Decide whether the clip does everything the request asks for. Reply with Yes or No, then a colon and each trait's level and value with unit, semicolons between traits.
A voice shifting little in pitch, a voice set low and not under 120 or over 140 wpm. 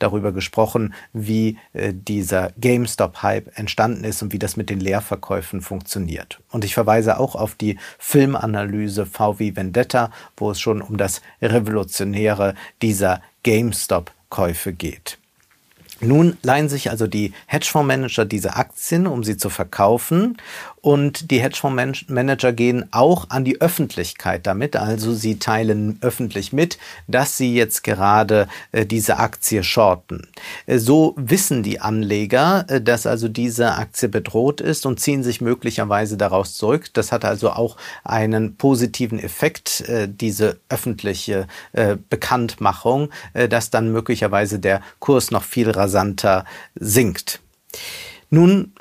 No: average, 3.5 semitones; low, 110 Hz; average, 135 wpm